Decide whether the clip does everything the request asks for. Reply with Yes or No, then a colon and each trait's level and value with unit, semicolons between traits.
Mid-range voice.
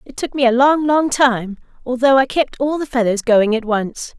No: very high, 255 Hz